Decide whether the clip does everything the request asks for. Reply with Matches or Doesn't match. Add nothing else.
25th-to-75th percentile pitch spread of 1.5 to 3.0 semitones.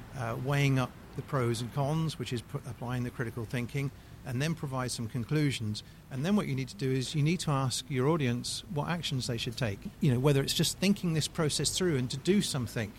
Doesn't match